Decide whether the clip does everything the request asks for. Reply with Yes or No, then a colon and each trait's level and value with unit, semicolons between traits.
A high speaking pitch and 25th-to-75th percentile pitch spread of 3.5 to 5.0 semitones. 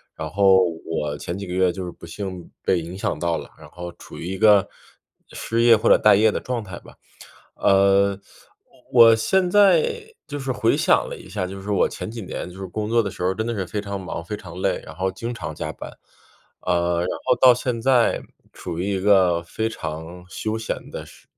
No: low, 100 Hz; average, 4.0 semitones